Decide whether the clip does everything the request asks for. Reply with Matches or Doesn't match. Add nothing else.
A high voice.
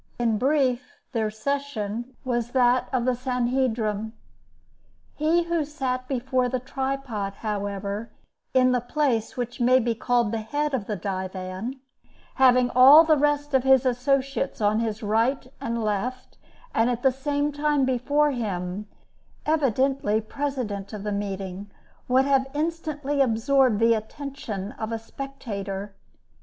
Matches